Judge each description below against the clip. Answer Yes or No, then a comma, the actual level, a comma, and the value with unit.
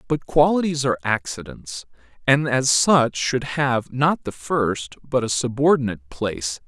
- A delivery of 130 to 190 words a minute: Yes, average, 145 wpm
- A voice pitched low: Yes, low, 125 Hz